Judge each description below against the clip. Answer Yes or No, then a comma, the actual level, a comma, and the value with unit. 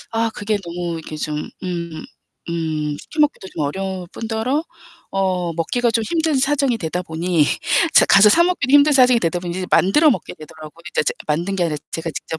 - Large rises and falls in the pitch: Yes, wide, 6.3 semitones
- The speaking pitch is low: No, medium, 185 Hz